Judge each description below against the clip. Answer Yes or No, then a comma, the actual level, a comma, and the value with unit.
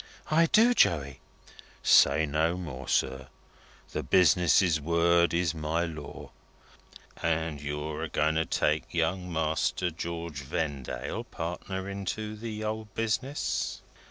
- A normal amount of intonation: Yes, average, 3.6 semitones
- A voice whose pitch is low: Yes, very low, 85 Hz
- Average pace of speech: No, slow, 120 wpm